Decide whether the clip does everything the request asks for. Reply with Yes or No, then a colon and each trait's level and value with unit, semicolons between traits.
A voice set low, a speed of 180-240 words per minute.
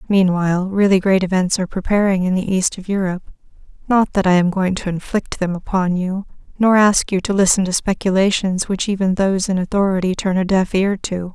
No: high, 190 Hz; average, 195 wpm